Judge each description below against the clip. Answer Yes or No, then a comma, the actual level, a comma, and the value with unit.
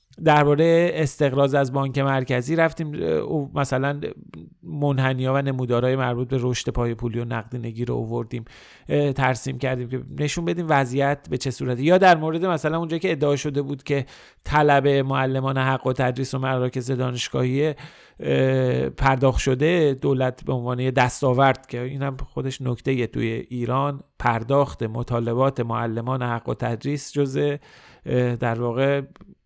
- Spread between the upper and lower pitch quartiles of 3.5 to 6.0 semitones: No, narrow, 2.5 semitones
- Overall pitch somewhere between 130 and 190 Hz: Yes, low, 135 Hz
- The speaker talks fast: No, average, 145 wpm